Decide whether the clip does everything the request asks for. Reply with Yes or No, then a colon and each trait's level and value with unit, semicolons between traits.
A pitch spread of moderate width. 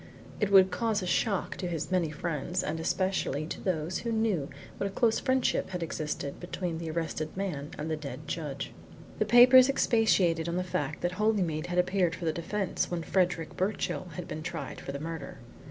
Yes: average, 3.7 semitones